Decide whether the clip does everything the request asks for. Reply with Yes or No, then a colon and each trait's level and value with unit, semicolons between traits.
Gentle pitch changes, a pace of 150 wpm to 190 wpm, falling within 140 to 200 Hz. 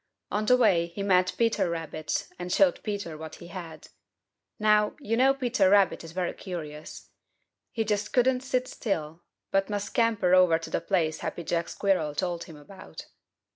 No: average, 4.1 semitones; average, 175 wpm; medium, 185 Hz